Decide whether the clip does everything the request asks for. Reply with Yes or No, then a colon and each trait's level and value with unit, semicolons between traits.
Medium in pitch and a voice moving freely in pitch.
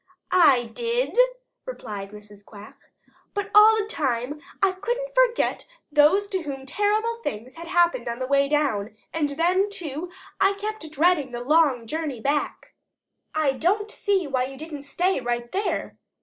No: very high, 310 Hz; wide, 7.4 semitones